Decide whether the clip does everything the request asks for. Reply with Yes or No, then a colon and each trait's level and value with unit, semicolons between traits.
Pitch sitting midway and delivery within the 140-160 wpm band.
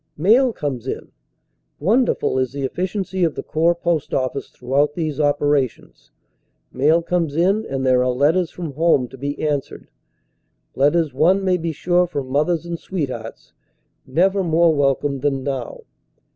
Yes: medium, 150 Hz; average, 155 wpm